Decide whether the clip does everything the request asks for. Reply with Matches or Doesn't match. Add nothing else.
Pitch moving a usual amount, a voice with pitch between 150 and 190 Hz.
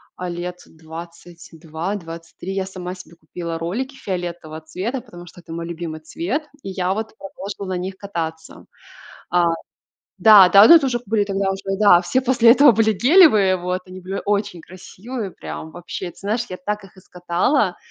Matches